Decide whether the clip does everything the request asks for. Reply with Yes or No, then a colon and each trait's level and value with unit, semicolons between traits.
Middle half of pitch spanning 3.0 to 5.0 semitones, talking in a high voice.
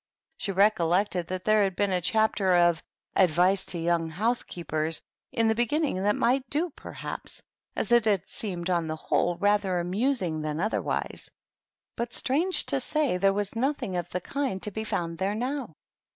Yes: average, 4.7 semitones; high, 195 Hz